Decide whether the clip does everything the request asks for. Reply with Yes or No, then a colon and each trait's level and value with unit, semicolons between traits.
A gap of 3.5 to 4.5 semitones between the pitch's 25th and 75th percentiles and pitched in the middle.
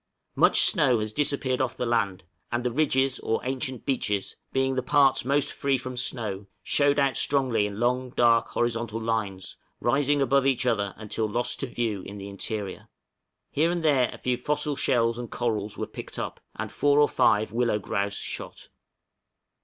No: average, 3.8 semitones; low, 125 Hz